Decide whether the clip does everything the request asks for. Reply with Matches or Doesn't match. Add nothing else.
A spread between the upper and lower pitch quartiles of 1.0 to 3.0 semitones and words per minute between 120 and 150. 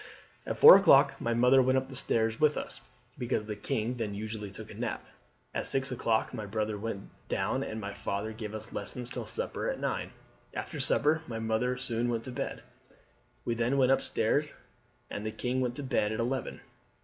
Doesn't match